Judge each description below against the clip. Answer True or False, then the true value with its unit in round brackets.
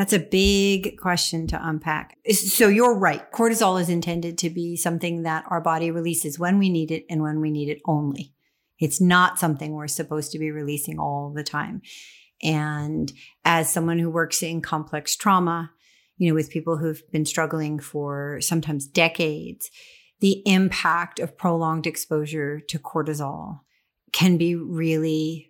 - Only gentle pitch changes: True (2.2 semitones)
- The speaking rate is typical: True (160 wpm)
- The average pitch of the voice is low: False (165 Hz)